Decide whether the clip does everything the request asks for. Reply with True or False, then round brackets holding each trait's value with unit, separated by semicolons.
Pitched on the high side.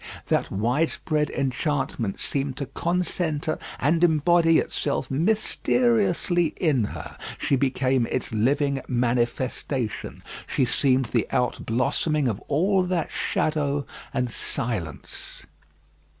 False (140 Hz)